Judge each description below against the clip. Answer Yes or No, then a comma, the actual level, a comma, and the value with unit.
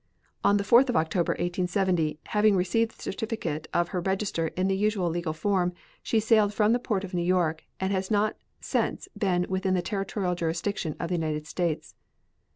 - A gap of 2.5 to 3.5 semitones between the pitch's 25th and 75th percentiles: Yes, average, 3.0 semitones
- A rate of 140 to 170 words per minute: No, average, 185 wpm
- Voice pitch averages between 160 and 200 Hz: Yes, medium, 185 Hz